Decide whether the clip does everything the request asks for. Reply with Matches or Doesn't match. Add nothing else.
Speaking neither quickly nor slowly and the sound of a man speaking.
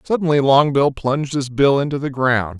Matches